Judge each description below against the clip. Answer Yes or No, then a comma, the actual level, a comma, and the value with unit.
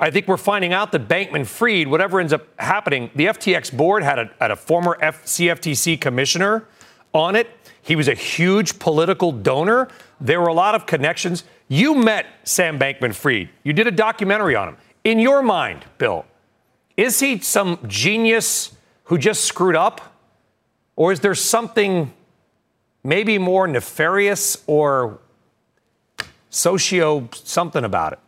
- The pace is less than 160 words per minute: Yes, average, 150 wpm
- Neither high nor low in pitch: Yes, medium, 180 Hz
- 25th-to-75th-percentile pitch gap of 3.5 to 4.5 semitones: No, average, 5.3 semitones